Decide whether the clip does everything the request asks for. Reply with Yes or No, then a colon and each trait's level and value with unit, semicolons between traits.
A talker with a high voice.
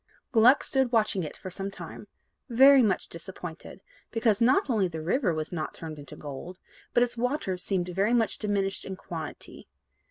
Yes: high, 200 Hz